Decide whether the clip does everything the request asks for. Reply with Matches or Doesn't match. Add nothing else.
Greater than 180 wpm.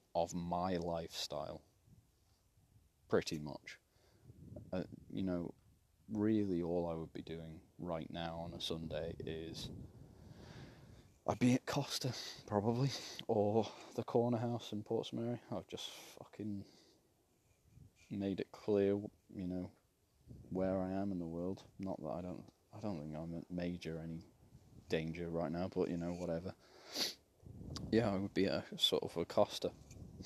Doesn't match